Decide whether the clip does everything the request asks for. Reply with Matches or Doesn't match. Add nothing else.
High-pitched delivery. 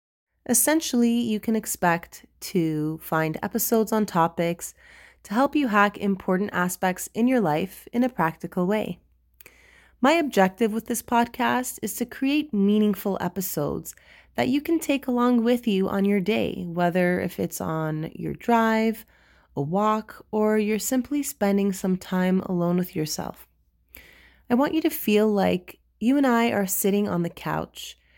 Matches